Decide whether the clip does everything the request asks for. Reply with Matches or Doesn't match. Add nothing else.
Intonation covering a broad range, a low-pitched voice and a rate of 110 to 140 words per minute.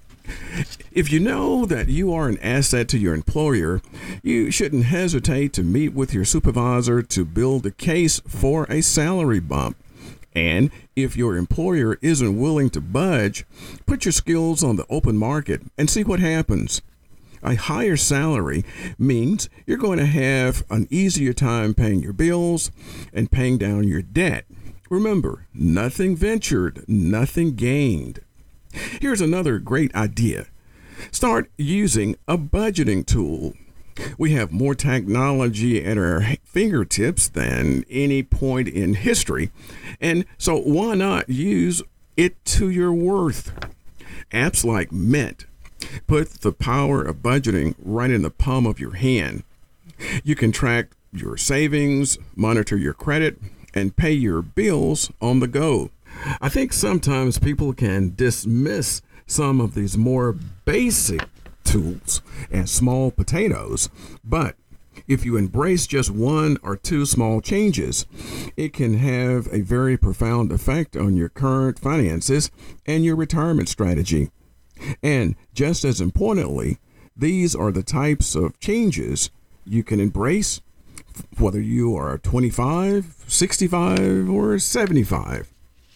Matches